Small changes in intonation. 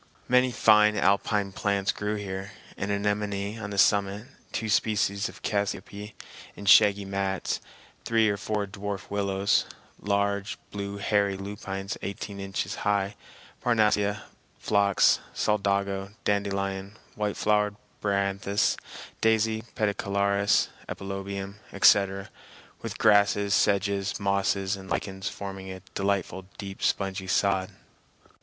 Yes: narrow, 0.9 semitones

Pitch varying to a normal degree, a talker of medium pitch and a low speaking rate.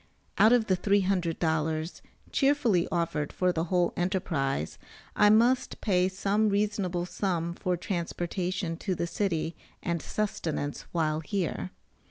Yes: average, 3.4 semitones; medium, 180 Hz; slow, 125 wpm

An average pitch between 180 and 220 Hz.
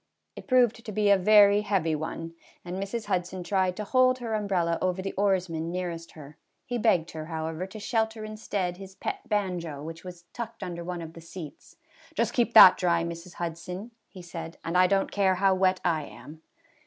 Yes: medium, 185 Hz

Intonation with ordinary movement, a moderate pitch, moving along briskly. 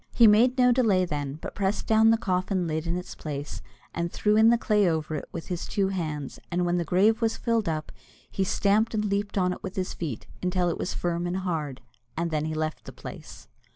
Yes: average, 4.2 semitones; medium, 180 Hz; fast, 230 wpm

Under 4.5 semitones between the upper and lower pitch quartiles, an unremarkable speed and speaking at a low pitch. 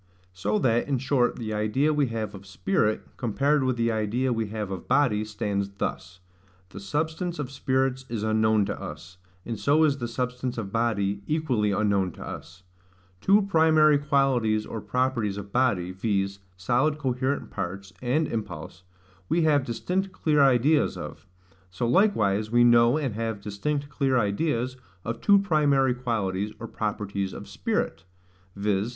No: average, 5.2 semitones; average, 155 wpm; low, 115 Hz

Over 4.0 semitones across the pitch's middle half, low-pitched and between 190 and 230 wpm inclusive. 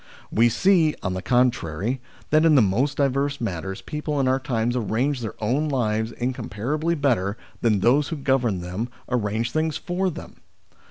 No: average, 4.8 semitones; low, 125 Hz; average, 165 wpm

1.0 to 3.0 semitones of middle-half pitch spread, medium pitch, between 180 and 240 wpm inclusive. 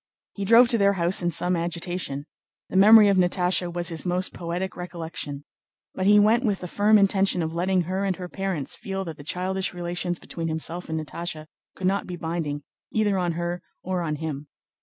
Yes: narrow, 2.4 semitones; medium, 180 Hz; average, 200 wpm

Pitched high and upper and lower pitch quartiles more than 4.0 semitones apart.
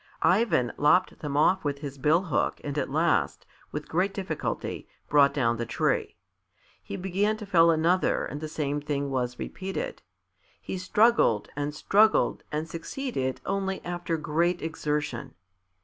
No: medium, 160 Hz; average, 4.5 semitones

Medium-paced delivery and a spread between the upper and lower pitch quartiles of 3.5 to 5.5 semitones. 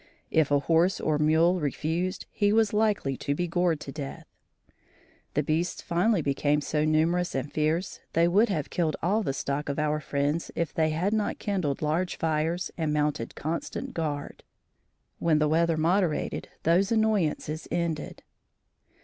No: average, 160 wpm; average, 2.9 semitones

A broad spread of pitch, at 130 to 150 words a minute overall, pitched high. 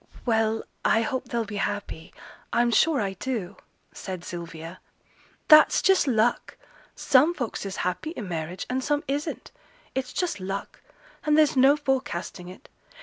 Yes: wide, 6.7 semitones; average, 145 wpm; high, 235 Hz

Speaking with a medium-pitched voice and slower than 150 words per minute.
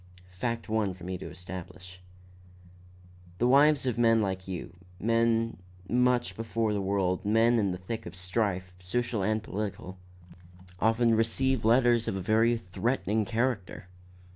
No: low, 110 Hz; average, 140 wpm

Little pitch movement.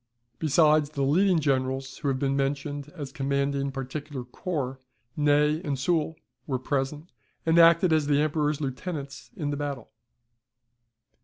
Yes: narrow, 2.1 semitones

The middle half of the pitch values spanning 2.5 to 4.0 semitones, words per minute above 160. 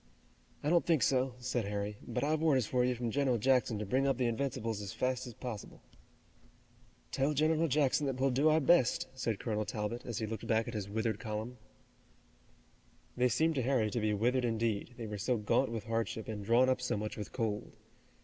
Yes: average, 3.3 semitones; fast, 205 wpm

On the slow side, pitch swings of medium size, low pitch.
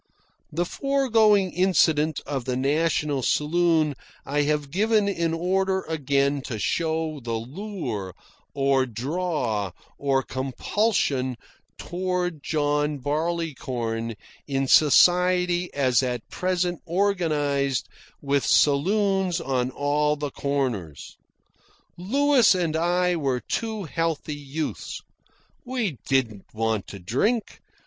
No: slow, 105 wpm; average, 5.0 semitones; medium, 150 Hz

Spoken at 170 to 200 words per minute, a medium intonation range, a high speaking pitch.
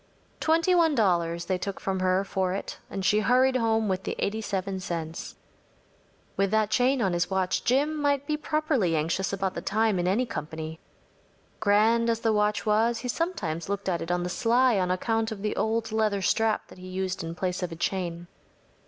Yes: average, 195 wpm; average, 3.9 semitones; high, 200 Hz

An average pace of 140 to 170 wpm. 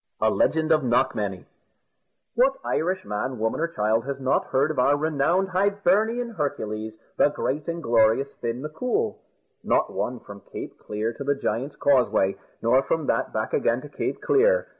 Yes: average, 165 wpm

